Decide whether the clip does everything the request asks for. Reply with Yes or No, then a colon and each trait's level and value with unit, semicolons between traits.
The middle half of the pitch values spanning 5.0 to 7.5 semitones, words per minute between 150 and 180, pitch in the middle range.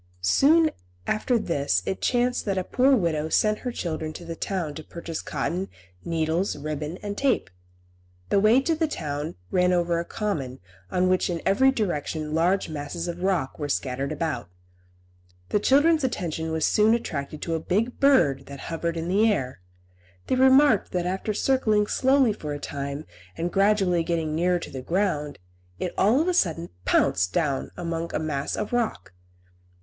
Yes: wide, 5.6 semitones; average, 175 wpm; medium, 175 Hz